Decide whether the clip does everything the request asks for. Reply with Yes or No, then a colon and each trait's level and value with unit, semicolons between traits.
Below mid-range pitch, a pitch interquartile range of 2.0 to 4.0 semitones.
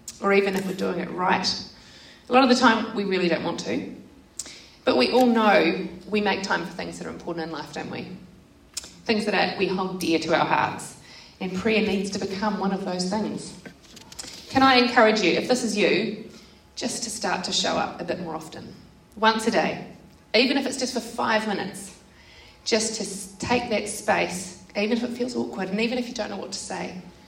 No: high, 205 Hz; average, 3.4 semitones